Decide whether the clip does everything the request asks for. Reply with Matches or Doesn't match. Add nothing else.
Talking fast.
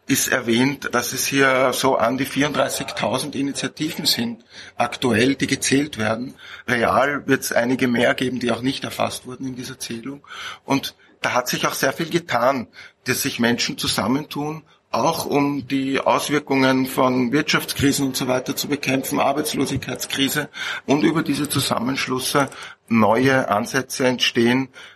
Doesn't match